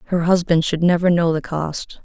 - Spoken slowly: No, fast, 205 wpm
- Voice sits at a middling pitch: Yes, medium, 170 Hz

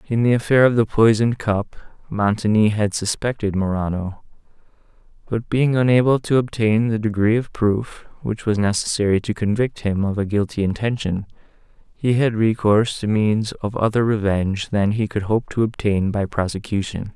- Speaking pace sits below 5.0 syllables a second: No, 5.1 syllables/s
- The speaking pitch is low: Yes, low, 110 Hz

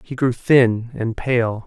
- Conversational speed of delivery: Yes, average, 180 wpm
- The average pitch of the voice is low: Yes, low, 120 Hz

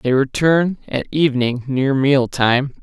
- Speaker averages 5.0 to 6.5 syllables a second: No, 4.0 syllables/s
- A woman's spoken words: No, male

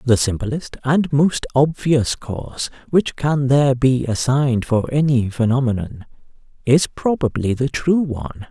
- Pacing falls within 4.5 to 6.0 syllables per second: No, 4.3 syllables/s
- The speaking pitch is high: No, low, 130 Hz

